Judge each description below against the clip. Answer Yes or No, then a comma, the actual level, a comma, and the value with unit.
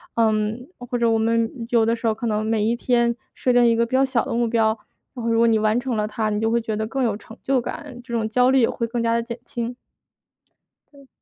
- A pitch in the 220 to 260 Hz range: Yes, high, 230 Hz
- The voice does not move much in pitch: Yes, narrow, 1.6 semitones